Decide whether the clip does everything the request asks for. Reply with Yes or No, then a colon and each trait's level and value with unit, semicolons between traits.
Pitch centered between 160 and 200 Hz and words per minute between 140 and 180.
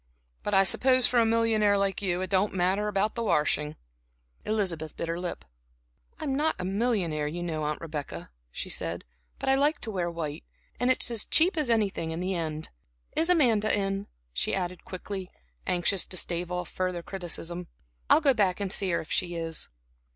No: high, 190 Hz; average, 190 wpm